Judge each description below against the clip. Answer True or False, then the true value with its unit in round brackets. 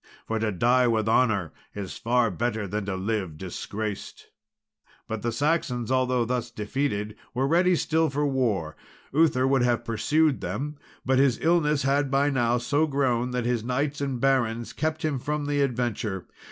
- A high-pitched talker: False (125 Hz)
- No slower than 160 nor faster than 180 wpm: True (165 wpm)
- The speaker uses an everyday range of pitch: True (4.1 semitones)